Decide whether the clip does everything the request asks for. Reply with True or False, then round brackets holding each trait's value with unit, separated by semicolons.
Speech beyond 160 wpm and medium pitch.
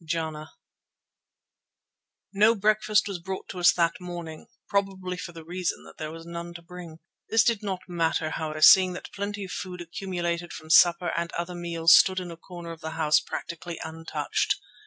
True (180 wpm; 175 Hz)